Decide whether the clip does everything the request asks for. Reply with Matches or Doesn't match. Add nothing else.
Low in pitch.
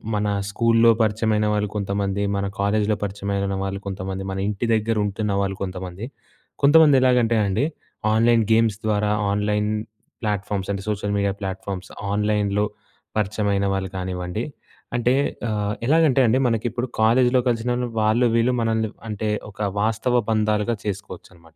Matches